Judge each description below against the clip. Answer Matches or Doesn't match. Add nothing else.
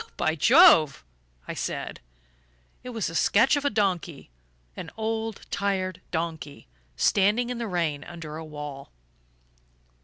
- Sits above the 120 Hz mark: Matches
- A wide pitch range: Matches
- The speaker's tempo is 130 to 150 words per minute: Matches